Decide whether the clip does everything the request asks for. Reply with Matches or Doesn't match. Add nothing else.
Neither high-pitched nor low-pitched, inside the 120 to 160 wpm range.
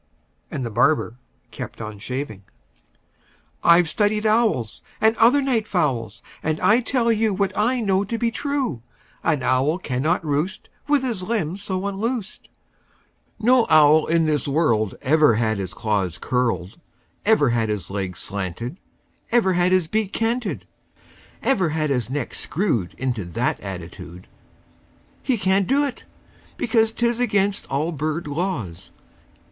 Matches